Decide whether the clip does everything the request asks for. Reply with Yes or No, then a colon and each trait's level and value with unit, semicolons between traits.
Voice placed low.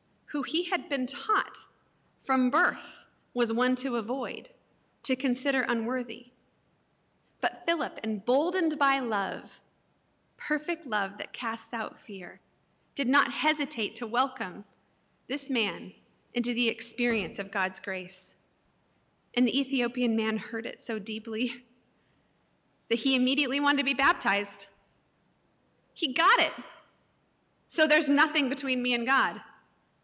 No: very high, 250 Hz